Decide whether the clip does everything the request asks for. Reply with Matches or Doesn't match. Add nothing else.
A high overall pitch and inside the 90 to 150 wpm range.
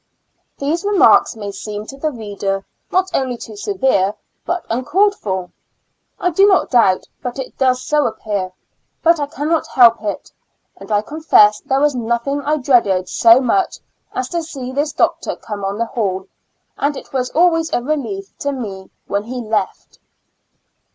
Doesn't match